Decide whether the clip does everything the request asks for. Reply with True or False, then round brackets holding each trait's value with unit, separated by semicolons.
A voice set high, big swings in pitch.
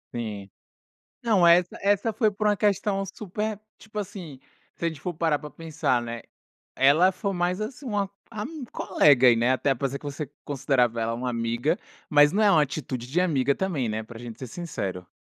False (155 Hz; 7.7 semitones)